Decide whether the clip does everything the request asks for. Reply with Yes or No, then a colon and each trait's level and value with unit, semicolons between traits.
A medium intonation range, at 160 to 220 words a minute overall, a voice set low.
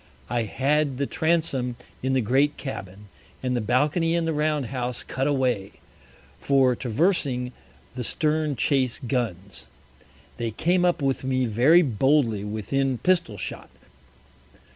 No: average, 3.9 semitones; slow, 135 wpm; low, 130 Hz